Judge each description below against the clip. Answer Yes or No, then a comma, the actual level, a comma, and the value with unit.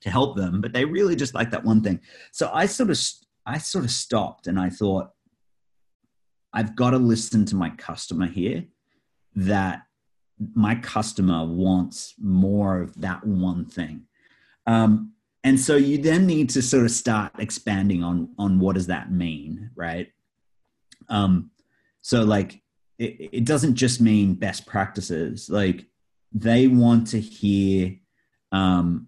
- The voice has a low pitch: Yes, low, 105 Hz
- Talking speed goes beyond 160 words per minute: No, average, 150 wpm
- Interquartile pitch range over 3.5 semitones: Yes, average, 4.2 semitones